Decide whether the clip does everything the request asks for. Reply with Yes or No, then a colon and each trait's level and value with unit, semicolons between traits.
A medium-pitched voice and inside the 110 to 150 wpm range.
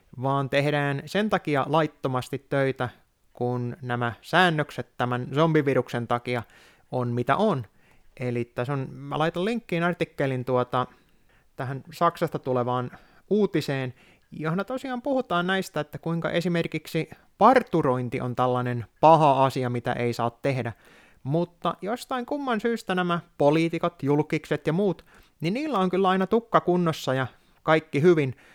Yes: medium, 150 Hz; average, 130 wpm